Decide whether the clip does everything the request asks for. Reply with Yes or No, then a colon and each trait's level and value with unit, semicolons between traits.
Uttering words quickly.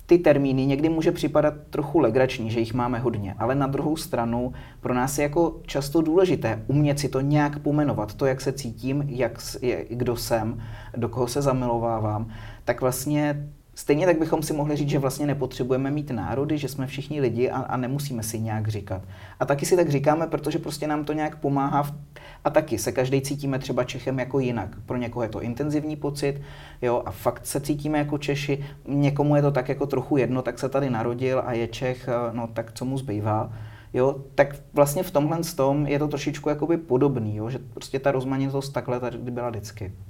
Yes: fast, 200 wpm